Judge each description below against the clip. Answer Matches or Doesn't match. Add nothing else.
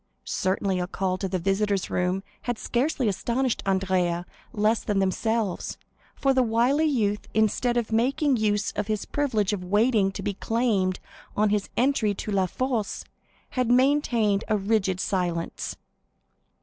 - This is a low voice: Doesn't match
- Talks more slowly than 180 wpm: Matches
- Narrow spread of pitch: Doesn't match